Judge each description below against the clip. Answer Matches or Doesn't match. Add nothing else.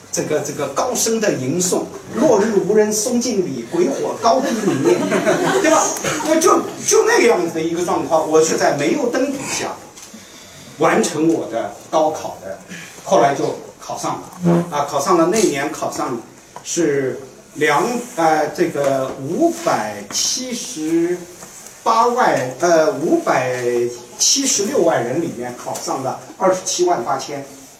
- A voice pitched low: Doesn't match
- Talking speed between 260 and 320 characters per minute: Doesn't match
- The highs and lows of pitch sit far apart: Matches